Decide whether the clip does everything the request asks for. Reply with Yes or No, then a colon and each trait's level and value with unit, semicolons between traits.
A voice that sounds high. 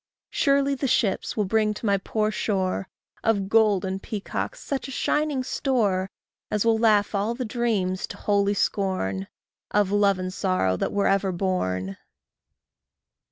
Yes: high, 205 Hz